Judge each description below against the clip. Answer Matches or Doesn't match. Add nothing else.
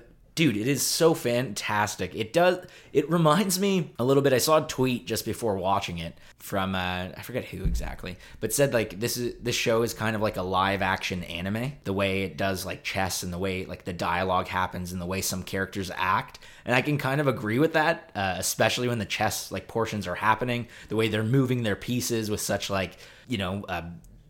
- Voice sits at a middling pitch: Doesn't match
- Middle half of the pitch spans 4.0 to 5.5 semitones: Matches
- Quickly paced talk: Matches